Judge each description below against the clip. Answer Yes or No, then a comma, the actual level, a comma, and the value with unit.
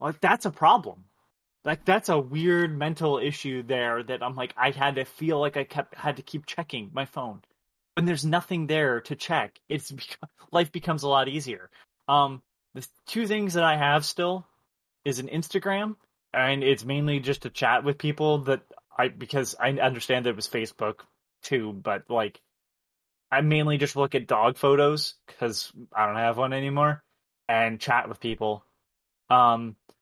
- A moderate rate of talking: Yes, average, 175 wpm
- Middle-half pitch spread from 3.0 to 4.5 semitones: Yes, average, 4.0 semitones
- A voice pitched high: No, medium, 140 Hz